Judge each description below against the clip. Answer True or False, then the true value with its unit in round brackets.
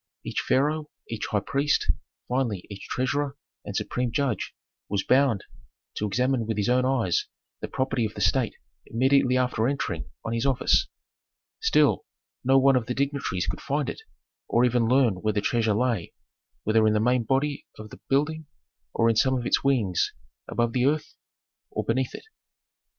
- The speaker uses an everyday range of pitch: True (3.6 semitones)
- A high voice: False (125 Hz)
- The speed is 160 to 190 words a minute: True (170 wpm)